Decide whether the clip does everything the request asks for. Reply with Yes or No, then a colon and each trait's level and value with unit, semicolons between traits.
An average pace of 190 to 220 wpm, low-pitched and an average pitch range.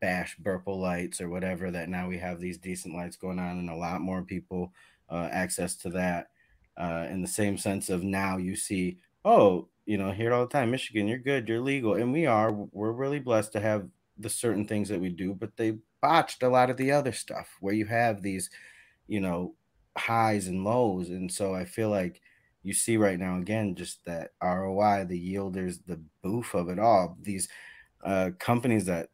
Yes: fast, 205 wpm; very low, 95 Hz; average, 3.3 semitones